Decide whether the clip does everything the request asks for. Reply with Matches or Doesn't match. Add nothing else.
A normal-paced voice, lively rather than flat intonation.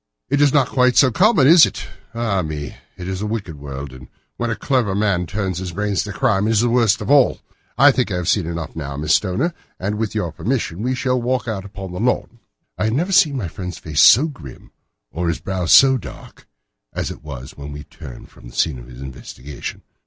Doesn't match